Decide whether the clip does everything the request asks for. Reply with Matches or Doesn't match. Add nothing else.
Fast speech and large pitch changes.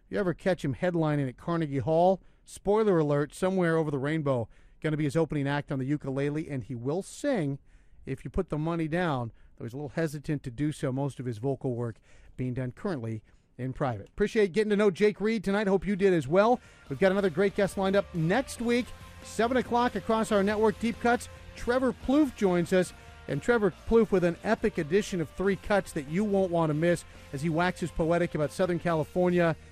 Matches